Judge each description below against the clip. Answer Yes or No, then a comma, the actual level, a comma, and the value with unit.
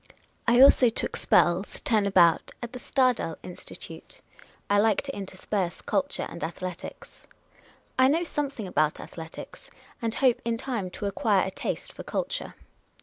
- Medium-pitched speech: No, high, 210 Hz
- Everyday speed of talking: Yes, average, 145 wpm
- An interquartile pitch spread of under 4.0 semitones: No, wide, 5.6 semitones